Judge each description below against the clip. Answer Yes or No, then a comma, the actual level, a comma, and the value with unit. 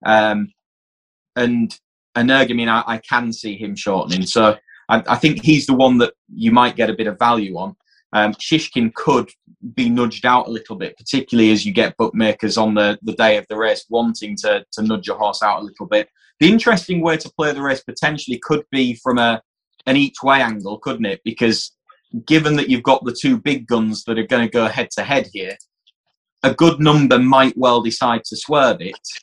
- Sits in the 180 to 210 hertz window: No, low, 120 Hz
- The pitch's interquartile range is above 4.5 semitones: Yes, average, 4.9 semitones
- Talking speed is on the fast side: Yes, fast, 210 wpm